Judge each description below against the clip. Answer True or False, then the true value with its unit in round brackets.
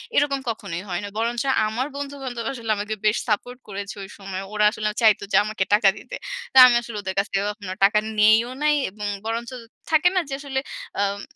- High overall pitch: True (215 Hz)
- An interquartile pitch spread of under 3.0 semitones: False (3.3 semitones)